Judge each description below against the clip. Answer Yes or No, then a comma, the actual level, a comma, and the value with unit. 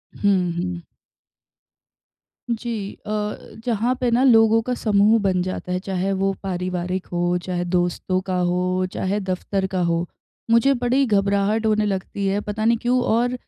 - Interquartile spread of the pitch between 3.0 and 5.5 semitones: Yes, average, 3.6 semitones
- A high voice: Yes, high, 195 Hz